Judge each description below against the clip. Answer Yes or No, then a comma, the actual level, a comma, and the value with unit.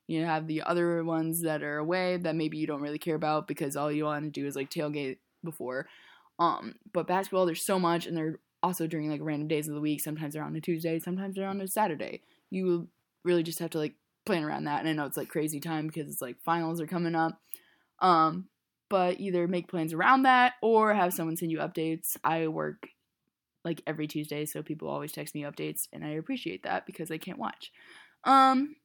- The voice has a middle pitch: Yes, medium, 160 Hz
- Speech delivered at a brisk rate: Yes, fast, 225 wpm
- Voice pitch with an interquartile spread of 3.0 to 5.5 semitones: No, narrow, 2.6 semitones